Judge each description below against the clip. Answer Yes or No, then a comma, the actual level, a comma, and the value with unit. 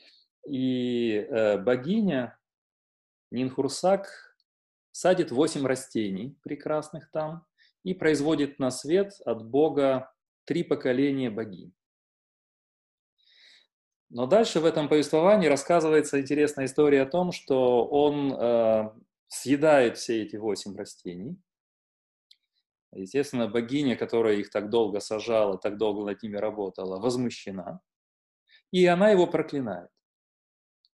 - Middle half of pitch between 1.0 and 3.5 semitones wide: No, wide, 5.4 semitones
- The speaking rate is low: Yes, slow, 100 wpm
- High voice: No, low, 135 Hz